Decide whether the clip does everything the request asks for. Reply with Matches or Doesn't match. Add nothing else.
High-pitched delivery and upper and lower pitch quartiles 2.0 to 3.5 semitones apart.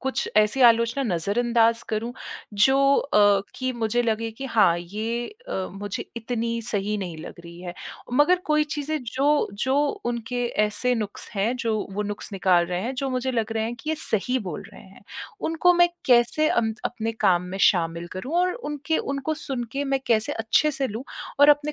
Doesn't match